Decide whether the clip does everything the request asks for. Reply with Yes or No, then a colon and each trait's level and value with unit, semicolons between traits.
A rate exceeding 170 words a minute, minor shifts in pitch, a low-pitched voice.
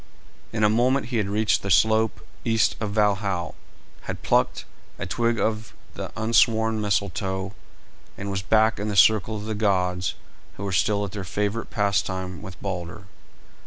No: average, 160 wpm; narrow, 2.3 semitones; low, 105 Hz